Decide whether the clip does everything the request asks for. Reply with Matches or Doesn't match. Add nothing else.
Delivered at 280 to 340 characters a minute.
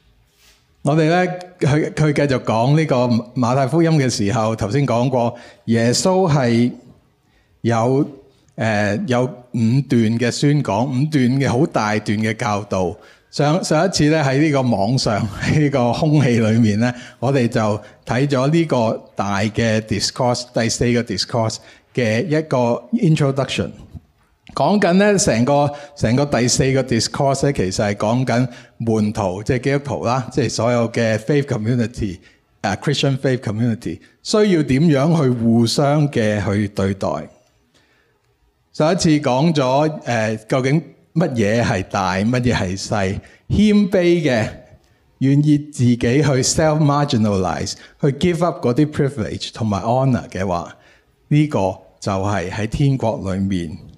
Matches